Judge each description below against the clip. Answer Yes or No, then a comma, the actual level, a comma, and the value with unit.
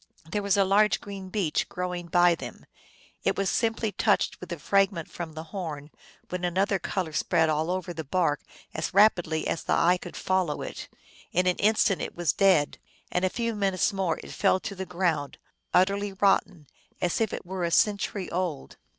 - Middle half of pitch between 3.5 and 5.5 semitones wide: No, average, 2.8 semitones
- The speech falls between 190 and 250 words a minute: Yes, average, 200 wpm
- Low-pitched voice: No, medium, 180 Hz